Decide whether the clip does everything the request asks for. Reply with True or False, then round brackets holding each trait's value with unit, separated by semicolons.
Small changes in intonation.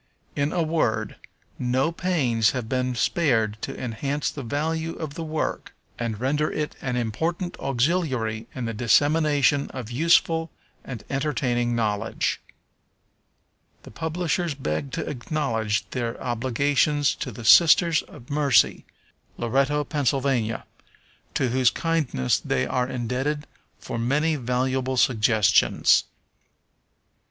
False (4.3 semitones)